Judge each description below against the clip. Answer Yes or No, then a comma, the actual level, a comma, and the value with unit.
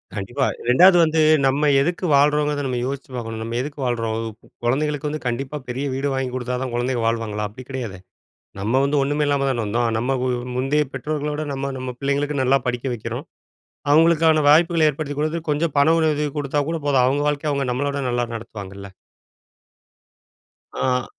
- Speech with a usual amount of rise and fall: Yes, average, 3.3 semitones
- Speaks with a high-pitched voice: No, low, 135 Hz